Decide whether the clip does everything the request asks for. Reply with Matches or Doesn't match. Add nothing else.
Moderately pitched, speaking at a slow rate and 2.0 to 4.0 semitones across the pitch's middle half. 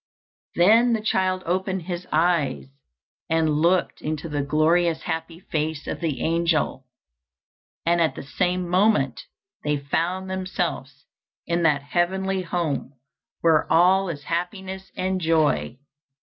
Matches